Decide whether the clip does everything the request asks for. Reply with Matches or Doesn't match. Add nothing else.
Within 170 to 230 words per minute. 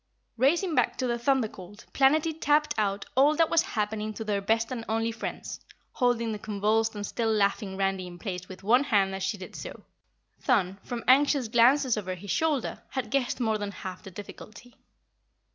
Matches